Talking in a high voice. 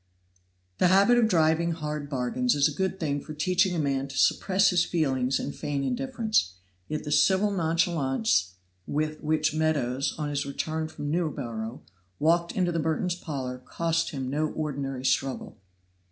No: medium, 155 Hz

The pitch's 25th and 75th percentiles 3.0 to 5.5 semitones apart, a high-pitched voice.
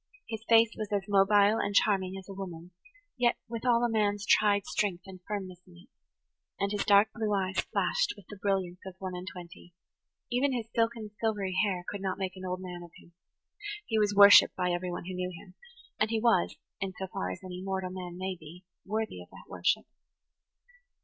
No: narrow, 2.5 semitones; high, 195 Hz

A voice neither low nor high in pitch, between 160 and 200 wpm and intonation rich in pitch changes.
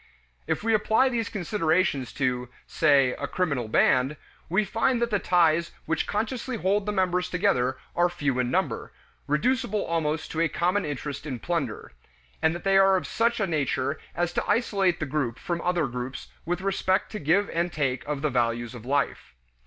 Yes: medium, 170 Hz; average, 185 wpm; wide, 5.8 semitones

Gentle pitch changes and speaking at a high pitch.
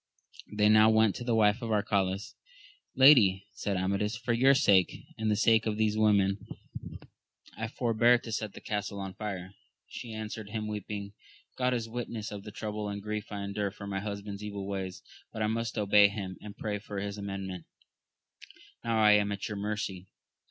No: narrow, 1.7 semitones; low, 105 Hz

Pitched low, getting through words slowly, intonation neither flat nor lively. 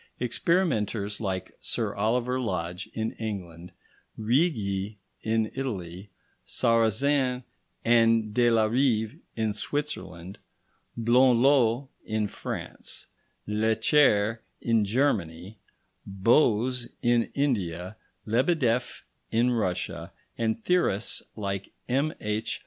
Yes: low, 110 Hz; slow, 85 wpm; average, 3.5 semitones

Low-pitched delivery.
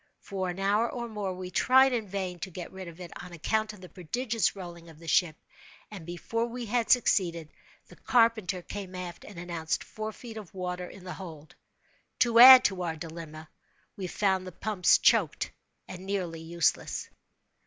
No: medium, 185 Hz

